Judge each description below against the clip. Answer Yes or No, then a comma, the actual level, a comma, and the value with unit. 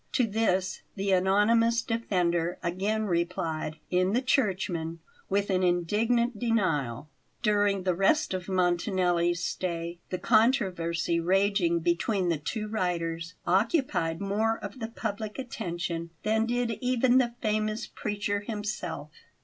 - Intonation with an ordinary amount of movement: Yes, average, 4.2 semitones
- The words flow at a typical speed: No, slow, 125 wpm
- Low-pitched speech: No, high, 195 Hz